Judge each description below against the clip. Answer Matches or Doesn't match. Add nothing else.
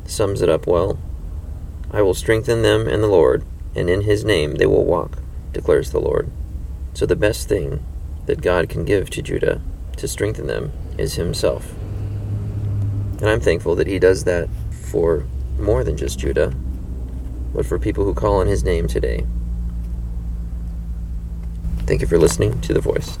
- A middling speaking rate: Matches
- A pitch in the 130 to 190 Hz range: Doesn't match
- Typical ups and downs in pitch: Doesn't match